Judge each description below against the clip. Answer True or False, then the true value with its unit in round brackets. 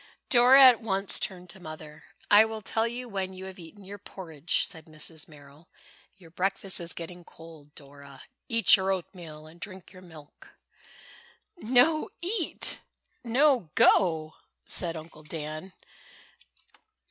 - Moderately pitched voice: True (180 Hz)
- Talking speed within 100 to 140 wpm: True (135 wpm)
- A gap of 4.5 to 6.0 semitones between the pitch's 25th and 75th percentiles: True (5.2 semitones)